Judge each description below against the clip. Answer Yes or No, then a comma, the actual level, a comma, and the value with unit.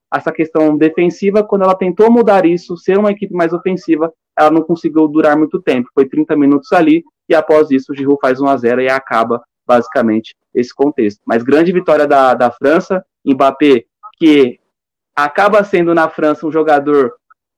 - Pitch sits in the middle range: Yes, medium, 155 Hz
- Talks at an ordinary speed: Yes, average, 165 wpm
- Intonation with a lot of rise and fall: No, average, 4.3 semitones